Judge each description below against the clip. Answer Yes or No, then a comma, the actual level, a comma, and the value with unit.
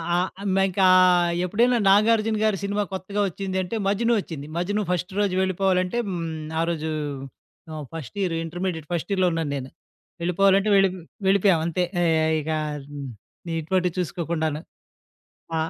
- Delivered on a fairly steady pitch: No, average, 3.3 semitones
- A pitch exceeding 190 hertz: No, medium, 185 Hz